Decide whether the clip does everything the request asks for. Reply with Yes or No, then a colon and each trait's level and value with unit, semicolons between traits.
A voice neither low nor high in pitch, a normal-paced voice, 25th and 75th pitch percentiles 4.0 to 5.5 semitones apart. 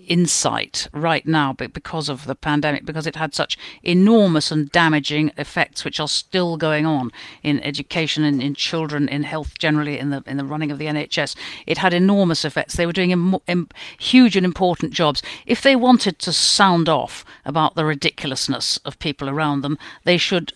No: medium, 155 Hz; average, 190 wpm; average, 3.1 semitones